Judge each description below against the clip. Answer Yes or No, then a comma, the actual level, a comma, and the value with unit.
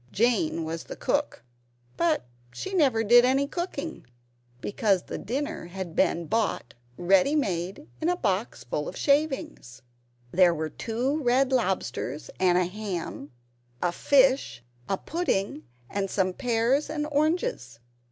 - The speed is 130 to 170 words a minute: Yes, slow, 135 wpm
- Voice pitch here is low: No, high, 225 Hz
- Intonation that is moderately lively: No, wide, 8.1 semitones